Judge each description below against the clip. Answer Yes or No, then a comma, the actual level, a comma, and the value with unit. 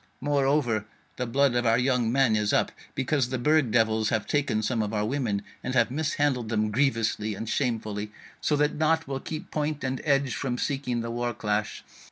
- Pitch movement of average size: Yes, average, 4.2 semitones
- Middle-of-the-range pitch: No, low, 125 Hz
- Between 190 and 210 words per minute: Yes, average, 195 wpm